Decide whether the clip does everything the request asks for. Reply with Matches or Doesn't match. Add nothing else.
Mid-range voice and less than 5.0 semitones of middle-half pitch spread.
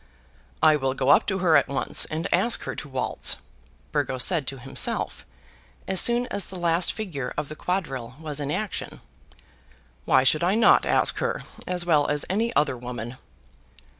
Doesn't match